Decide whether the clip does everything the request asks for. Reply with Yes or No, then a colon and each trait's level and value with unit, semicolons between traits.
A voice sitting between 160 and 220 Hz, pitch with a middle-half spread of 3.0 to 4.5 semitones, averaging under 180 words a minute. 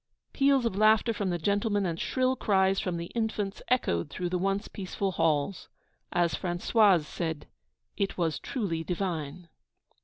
Yes: high, 190 Hz; average, 3.7 semitones; average, 150 wpm